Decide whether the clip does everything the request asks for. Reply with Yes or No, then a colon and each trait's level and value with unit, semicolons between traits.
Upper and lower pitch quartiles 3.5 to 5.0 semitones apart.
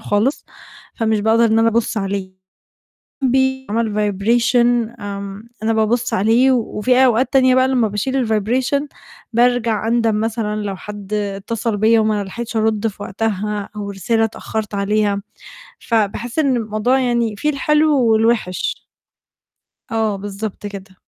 No: narrow, 2.6 semitones